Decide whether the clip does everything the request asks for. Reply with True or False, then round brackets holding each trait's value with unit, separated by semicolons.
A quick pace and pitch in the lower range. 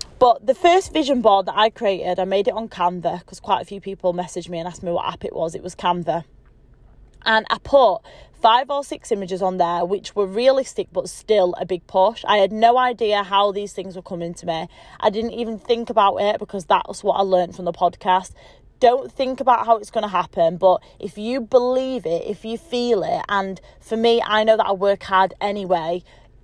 False (225 wpm; 195 Hz)